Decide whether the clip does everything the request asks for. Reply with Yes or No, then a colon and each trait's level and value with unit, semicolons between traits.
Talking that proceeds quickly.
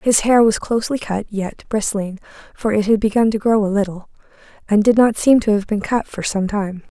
Yes: fast, 225 wpm